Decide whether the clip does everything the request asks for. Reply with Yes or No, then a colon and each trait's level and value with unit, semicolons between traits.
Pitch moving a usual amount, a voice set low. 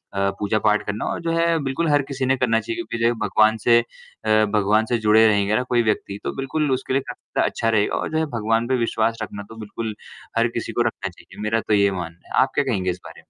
Yes: average, 3.7 semitones; low, 115 Hz